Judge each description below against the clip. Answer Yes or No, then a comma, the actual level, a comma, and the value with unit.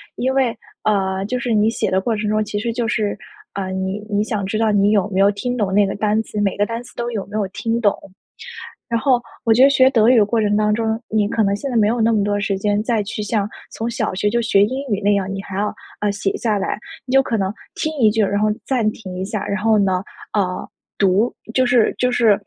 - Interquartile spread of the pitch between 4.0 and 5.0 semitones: No, narrow, 2.4 semitones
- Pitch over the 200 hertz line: Yes, high, 210 Hz